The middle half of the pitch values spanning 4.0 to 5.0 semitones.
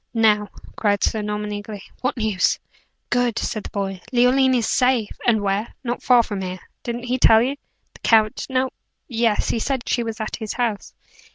No: average, 2.8 semitones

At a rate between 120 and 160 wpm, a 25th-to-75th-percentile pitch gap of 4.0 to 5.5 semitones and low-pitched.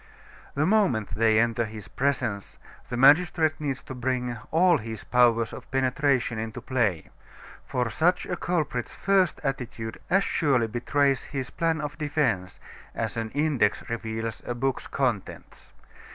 Yes: average, 140 wpm; average, 4.6 semitones; low, 130 Hz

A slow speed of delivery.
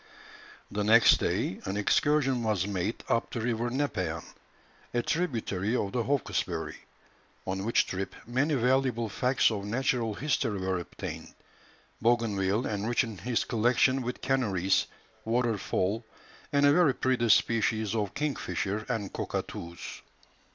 Yes: slow, 125 wpm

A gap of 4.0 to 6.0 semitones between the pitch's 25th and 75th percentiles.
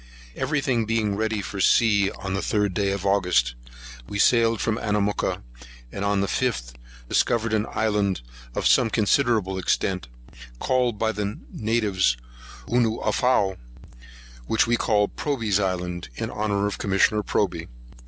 No: narrow, 2.6 semitones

